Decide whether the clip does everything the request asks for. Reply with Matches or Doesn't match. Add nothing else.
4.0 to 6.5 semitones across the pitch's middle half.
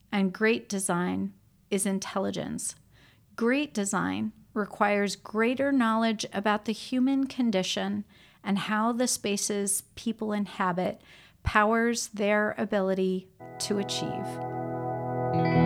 Doesn't match